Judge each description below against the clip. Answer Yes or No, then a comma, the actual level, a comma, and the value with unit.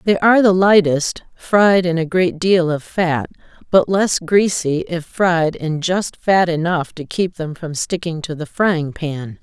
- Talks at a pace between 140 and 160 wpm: No, average, 185 wpm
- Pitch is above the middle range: No, medium, 175 Hz